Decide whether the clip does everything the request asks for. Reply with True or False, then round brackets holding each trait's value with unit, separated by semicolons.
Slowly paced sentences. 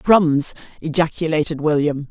True (85 wpm)